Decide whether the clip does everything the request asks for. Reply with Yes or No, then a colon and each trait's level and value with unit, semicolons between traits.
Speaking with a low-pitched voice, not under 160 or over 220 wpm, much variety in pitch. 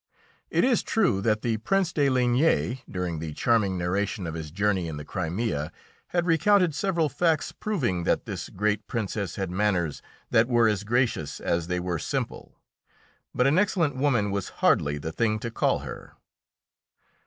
Yes: low, 110 Hz; average, 165 wpm; wide, 7.5 semitones